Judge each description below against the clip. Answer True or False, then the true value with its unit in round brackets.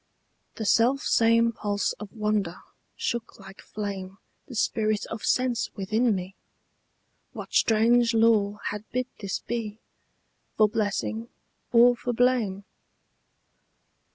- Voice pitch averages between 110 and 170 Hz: False (220 Hz)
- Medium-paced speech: False (115 wpm)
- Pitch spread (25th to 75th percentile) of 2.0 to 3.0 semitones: True (2.4 semitones)